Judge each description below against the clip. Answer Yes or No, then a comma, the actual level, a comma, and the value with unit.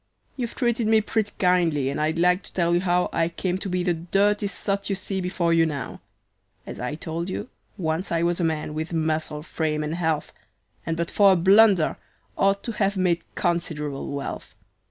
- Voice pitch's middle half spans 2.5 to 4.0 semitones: Yes, average, 3.4 semitones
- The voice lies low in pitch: No, medium, 175 Hz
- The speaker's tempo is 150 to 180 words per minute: No, average, 195 wpm